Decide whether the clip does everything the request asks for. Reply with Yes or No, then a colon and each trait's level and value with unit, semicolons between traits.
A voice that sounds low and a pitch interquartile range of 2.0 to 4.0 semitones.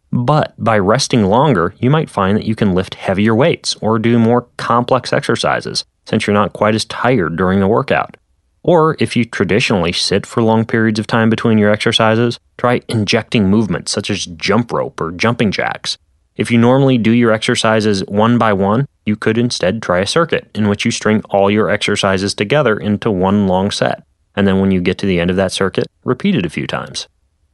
Yes: low, 110 Hz; average, 3.0 semitones